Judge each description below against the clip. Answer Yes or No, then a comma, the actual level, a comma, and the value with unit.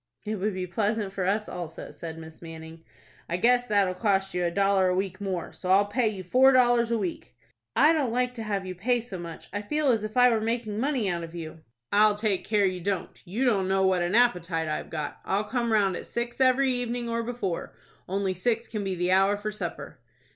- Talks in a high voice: Yes, high, 205 Hz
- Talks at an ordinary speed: No, fast, 230 wpm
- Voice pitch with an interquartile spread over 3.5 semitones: Yes, average, 4.2 semitones